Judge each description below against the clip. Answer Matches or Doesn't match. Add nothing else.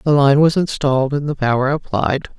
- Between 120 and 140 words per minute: Doesn't match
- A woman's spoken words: Matches